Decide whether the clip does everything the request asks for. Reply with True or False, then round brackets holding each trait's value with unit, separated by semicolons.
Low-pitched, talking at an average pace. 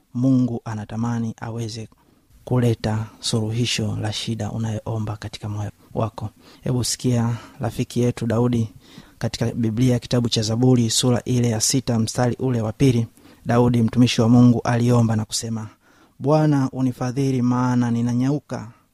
True (120 Hz; 125 wpm)